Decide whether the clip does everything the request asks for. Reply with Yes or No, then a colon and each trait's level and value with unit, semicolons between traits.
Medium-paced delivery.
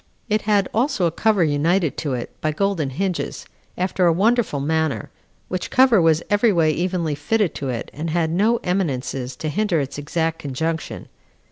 Yes: average, 170 wpm